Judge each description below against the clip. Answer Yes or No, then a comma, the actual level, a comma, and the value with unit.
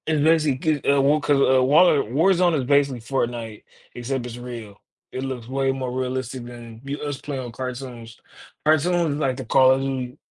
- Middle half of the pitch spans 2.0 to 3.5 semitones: Yes, average, 2.7 semitones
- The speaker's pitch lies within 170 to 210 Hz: No, low, 130 Hz